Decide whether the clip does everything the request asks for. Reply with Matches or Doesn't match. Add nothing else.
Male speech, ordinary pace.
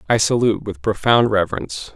Matches